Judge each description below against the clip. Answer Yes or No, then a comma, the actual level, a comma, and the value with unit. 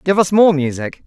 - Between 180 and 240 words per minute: Yes, fast, 225 wpm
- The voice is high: No, medium, 165 Hz